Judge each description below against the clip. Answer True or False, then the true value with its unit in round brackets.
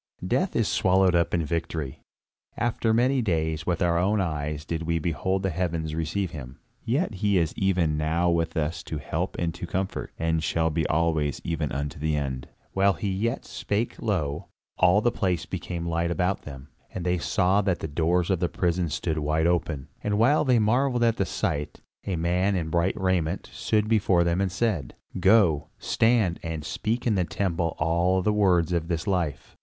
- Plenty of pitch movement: False (3.4 semitones)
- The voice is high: False (85 Hz)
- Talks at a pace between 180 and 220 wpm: True (190 wpm)